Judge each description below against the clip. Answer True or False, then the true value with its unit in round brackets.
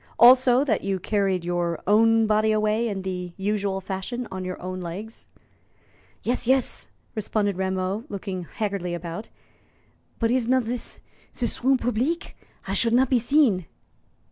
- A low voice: False (210 Hz)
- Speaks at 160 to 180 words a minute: False (145 wpm)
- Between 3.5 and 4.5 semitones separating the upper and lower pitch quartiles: True (4.1 semitones)